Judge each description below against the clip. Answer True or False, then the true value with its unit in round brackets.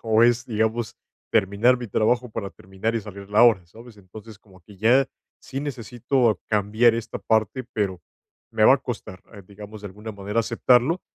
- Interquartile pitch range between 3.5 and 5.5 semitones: False (2.8 semitones)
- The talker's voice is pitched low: True (110 Hz)